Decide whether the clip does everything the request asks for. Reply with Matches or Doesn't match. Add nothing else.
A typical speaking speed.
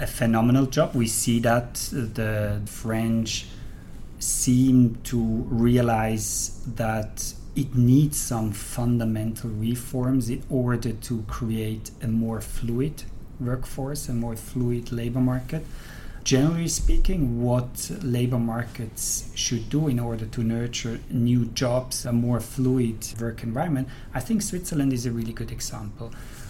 Doesn't match